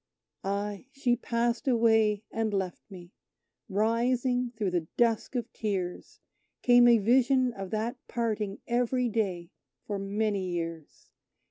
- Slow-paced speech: Yes, slow, 125 wpm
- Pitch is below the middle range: No, high, 220 Hz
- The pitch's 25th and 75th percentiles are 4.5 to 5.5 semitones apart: No, average, 3.6 semitones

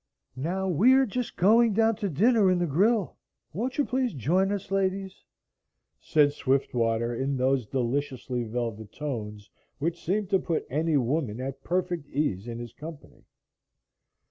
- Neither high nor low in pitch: Yes, medium, 155 Hz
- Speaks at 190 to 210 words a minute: No, average, 150 wpm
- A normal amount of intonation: No, wide, 7.4 semitones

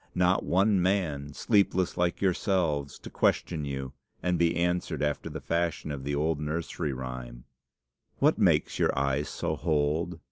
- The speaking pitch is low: Yes, very low, 80 Hz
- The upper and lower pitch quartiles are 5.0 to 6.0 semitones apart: No, average, 3.7 semitones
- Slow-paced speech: No, average, 150 wpm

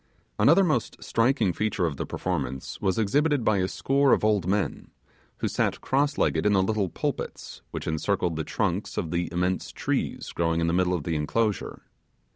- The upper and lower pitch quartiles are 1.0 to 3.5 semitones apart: No, average, 5.0 semitones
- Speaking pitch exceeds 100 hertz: No, very low, 95 Hz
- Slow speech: No, average, 185 wpm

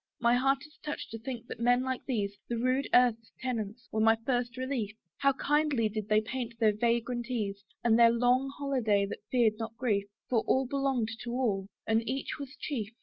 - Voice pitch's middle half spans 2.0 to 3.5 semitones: Yes, average, 2.9 semitones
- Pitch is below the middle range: No, high, 240 Hz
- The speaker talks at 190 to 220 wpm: Yes, average, 200 wpm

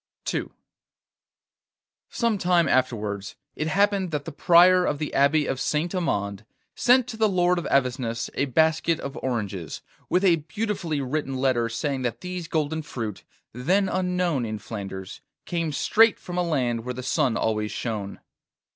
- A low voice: No, medium, 150 Hz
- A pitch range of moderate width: No, wide, 6.8 semitones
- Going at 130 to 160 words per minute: Yes, average, 155 wpm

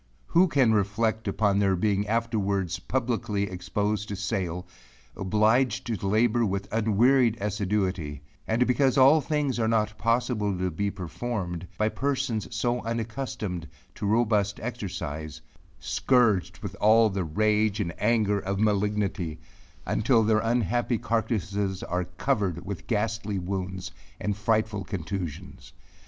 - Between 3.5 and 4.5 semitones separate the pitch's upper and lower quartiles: No, average, 3.0 semitones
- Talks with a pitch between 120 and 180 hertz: No, low, 105 Hz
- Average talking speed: No, slow, 125 wpm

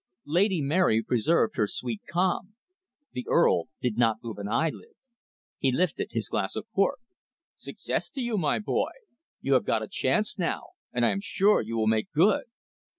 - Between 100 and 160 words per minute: No, average, 175 wpm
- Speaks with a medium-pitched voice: Yes, medium, 150 Hz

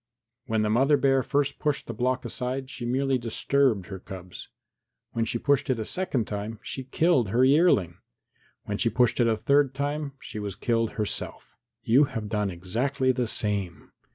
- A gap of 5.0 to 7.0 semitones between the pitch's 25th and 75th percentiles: No, average, 4.3 semitones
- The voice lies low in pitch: Yes, low, 120 Hz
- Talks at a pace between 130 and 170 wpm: No, average, 180 wpm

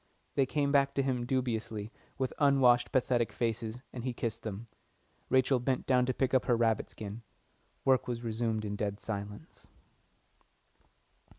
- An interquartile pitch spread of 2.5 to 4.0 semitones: Yes, average, 2.8 semitones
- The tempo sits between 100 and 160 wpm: Yes, average, 155 wpm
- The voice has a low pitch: Yes, low, 120 Hz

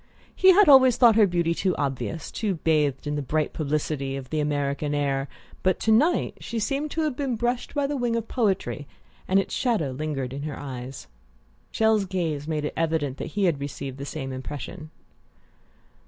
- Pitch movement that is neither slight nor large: No, wide, 7.8 semitones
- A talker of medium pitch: Yes, medium, 160 Hz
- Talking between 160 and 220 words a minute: Yes, average, 190 wpm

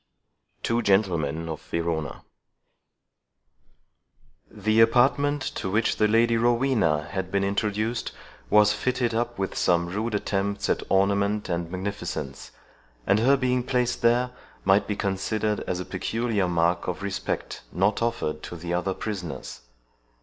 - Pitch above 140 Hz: No, low, 100 Hz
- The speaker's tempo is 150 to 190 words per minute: No, slow, 135 wpm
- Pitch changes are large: No, average, 4.0 semitones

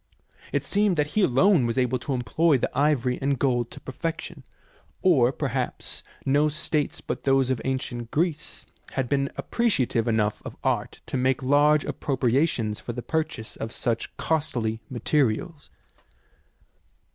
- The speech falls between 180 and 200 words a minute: No, average, 145 wpm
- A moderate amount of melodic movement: Yes, average, 3.9 semitones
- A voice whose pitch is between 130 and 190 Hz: Yes, low, 135 Hz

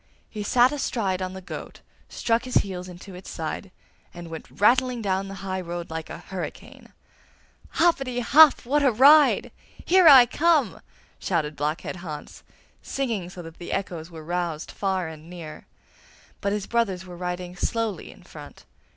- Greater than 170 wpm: No, average, 160 wpm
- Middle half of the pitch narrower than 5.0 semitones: No, wide, 5.6 semitones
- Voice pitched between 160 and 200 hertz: Yes, high, 190 Hz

